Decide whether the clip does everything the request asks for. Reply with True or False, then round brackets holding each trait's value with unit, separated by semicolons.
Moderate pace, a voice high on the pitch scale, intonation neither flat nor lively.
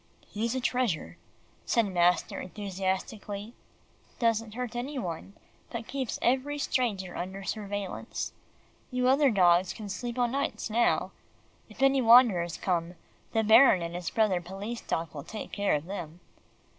True (145 wpm; 210 Hz; 4.8 semitones)